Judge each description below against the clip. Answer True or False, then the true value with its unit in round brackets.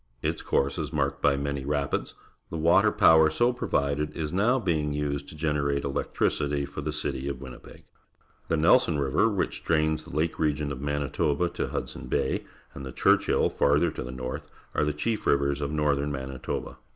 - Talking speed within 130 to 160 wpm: False (175 wpm)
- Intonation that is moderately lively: False (2.0 semitones)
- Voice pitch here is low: True (75 Hz)